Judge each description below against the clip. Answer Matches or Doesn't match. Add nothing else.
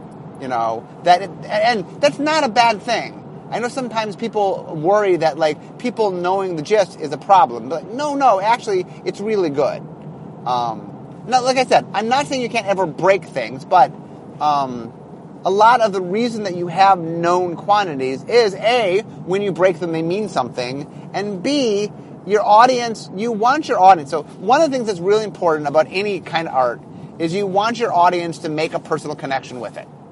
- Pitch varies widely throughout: Matches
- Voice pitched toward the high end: Matches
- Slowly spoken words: Doesn't match